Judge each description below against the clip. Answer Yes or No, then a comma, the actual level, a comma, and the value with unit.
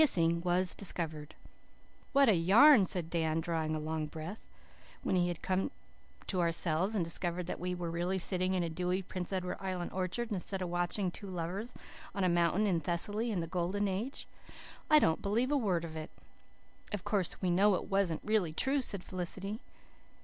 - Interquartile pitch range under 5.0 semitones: Yes, average, 2.9 semitones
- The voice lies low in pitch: No, medium, 180 Hz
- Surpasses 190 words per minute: No, average, 185 wpm